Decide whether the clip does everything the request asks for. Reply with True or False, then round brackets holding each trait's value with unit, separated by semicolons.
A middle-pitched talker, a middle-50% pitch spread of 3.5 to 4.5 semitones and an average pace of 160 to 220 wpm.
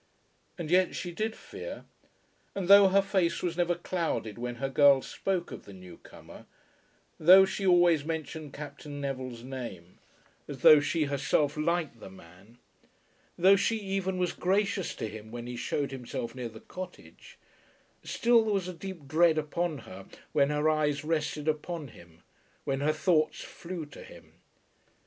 False (155 Hz; 5.2 semitones; 165 wpm)